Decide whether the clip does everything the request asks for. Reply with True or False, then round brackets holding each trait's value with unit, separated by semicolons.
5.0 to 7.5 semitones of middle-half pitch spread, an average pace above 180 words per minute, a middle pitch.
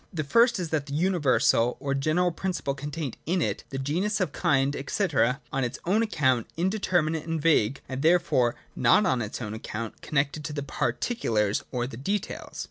True (5.3 semitones; 190 wpm; 150 Hz)